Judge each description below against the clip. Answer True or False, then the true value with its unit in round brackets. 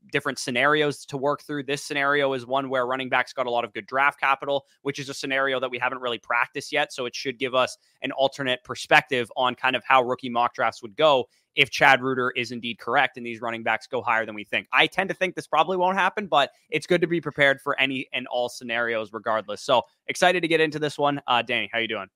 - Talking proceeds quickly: True (250 wpm)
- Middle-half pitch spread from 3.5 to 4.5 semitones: False (2.8 semitones)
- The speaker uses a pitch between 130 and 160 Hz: True (135 Hz)